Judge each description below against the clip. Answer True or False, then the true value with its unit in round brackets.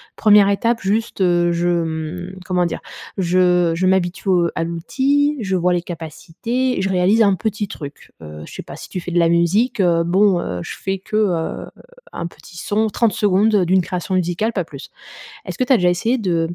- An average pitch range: True (3.4 semitones)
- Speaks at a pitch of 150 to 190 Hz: True (185 Hz)